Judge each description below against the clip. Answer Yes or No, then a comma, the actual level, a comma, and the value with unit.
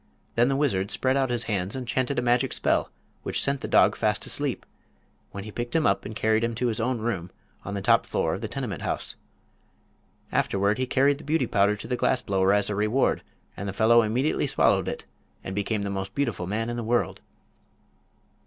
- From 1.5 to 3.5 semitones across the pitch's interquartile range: No, average, 4.0 semitones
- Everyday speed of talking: No, fast, 215 wpm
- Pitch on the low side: Yes, low, 115 Hz